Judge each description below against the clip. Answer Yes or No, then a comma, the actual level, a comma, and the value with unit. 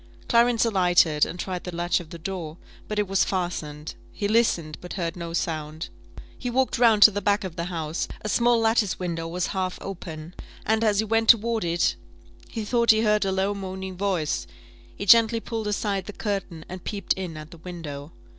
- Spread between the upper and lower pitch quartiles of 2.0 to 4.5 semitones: Yes, average, 4.2 semitones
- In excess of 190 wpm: Yes, average, 200 wpm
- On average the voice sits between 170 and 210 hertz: Yes, high, 190 Hz